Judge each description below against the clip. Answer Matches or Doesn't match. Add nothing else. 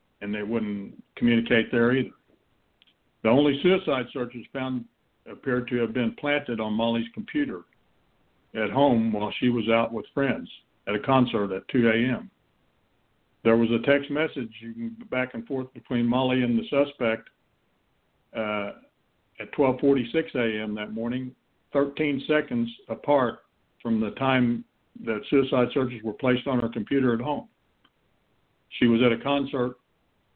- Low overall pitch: Matches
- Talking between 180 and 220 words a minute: Doesn't match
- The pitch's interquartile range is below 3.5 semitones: Matches